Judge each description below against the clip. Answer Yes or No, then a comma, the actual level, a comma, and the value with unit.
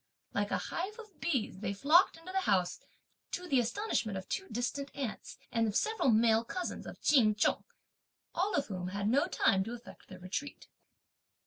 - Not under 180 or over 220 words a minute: Yes, average, 185 wpm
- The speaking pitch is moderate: No, high, 240 Hz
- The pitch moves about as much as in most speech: No, wide, 8.8 semitones